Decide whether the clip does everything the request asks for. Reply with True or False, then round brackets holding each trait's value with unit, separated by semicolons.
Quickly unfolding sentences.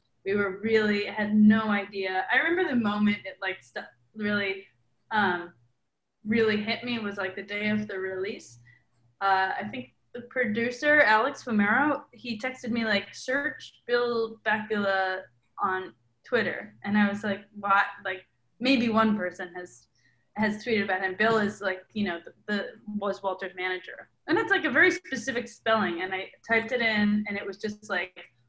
False (175 wpm)